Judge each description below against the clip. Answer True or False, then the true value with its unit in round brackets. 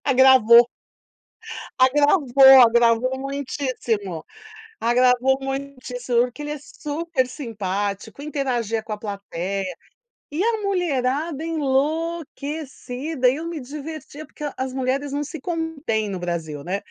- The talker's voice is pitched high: True (265 Hz)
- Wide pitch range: False (4.1 semitones)